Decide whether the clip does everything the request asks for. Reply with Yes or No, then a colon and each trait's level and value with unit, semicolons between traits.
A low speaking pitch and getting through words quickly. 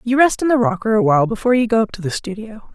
No: high, 225 Hz; fast, 285 wpm